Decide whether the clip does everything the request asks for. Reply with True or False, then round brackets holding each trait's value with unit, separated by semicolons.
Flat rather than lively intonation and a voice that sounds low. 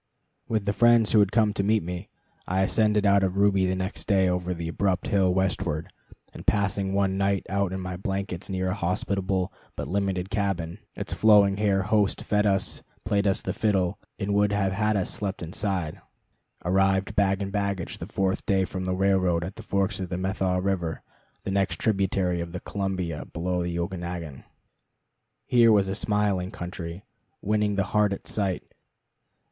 True (1.7 semitones; 95 Hz)